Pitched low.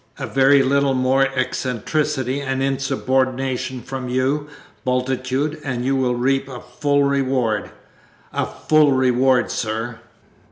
Yes: low, 130 Hz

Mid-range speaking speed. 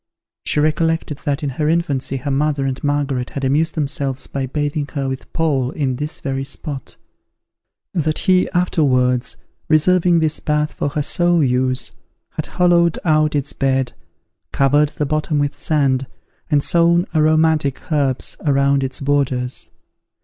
Yes: average, 145 wpm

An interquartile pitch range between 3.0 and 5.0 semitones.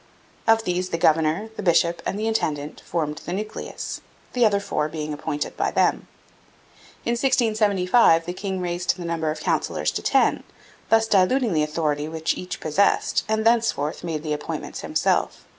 No: wide, 5.6 semitones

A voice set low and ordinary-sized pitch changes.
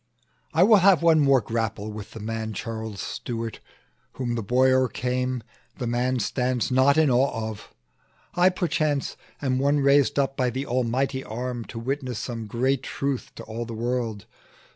Yes: low, 125 Hz; average, 3.1 semitones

